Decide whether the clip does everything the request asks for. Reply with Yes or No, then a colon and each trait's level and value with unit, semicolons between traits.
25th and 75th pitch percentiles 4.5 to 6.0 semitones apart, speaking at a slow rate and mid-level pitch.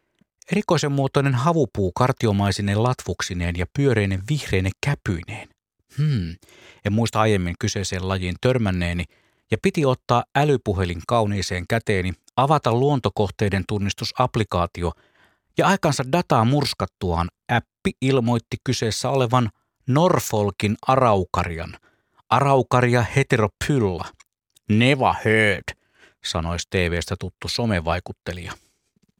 No: wide, 5.6 semitones; slow, 90 wpm; low, 110 Hz